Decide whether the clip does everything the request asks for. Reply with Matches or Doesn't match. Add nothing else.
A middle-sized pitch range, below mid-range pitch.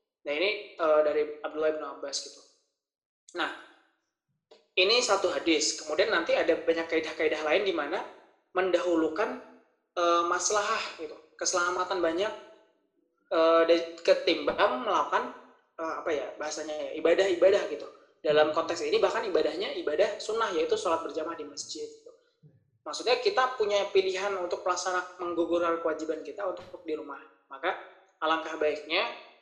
Doesn't match